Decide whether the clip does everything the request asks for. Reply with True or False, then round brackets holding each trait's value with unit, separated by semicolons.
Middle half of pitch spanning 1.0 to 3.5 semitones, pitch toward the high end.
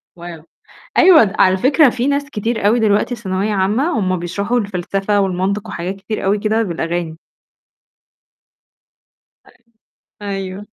True (3.1 semitones; 200 Hz)